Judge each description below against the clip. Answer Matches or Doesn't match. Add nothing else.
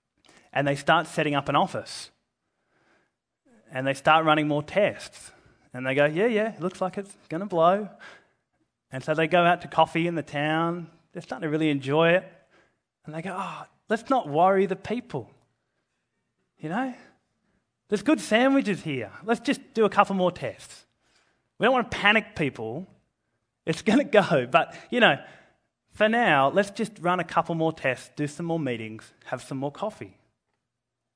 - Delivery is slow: Doesn't match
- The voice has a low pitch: Doesn't match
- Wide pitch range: Matches